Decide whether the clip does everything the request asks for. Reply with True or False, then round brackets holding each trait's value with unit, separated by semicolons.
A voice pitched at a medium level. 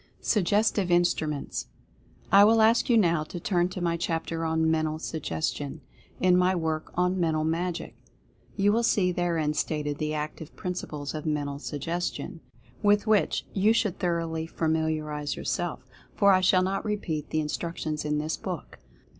True (165 Hz)